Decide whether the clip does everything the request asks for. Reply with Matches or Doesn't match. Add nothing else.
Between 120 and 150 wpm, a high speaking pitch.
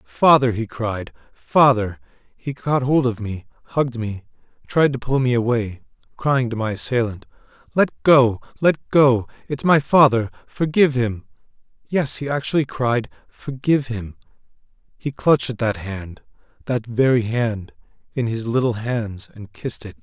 Doesn't match